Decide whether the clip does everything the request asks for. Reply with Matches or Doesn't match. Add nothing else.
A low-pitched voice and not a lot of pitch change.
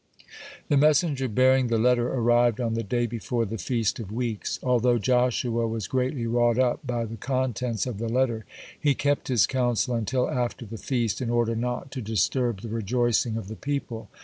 Matches